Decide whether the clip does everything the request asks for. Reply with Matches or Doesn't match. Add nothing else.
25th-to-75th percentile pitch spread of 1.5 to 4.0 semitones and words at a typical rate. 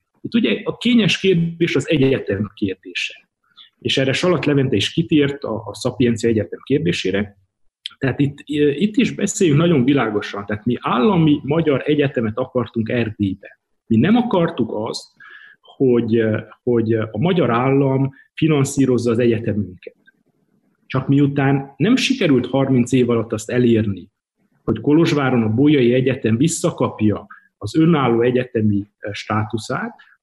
Doesn't match